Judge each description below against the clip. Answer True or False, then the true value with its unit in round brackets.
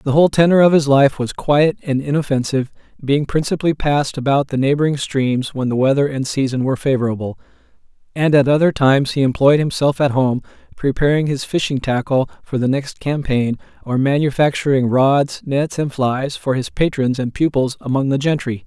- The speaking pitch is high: False (140 Hz)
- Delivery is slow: False (175 wpm)